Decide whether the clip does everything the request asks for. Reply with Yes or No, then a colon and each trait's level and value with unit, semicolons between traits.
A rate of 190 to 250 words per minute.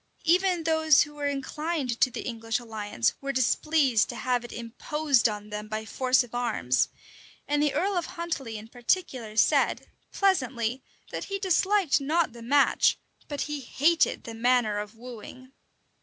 No: average, 160 wpm